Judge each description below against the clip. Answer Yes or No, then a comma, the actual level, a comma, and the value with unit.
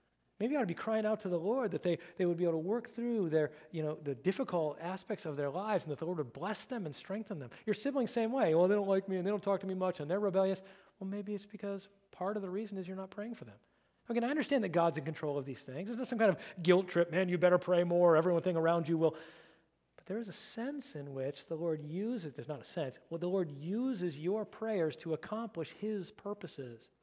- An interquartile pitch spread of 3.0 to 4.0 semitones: No, average, 4.5 semitones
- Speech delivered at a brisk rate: Yes, fast, 270 wpm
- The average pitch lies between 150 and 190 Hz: Yes, medium, 185 Hz